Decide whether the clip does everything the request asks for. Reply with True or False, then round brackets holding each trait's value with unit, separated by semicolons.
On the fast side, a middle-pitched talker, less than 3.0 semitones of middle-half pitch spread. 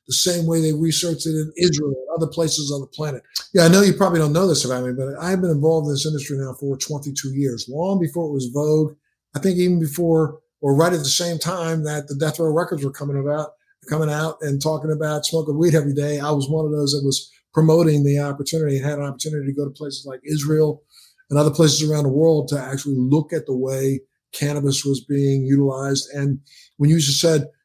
True (235 wpm; 150 Hz; 2.4 semitones)